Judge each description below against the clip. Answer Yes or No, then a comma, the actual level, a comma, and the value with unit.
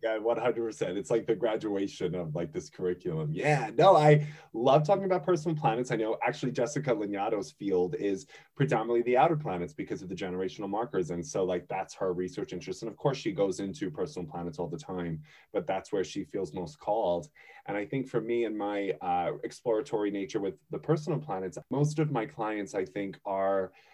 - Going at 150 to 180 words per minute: No, fast, 205 wpm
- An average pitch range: No, wide, 8.2 semitones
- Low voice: Yes, low, 110 Hz